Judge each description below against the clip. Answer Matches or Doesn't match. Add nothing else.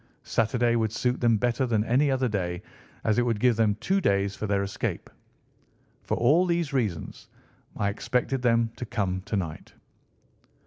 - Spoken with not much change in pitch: Doesn't match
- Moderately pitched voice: Doesn't match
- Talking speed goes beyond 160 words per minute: Matches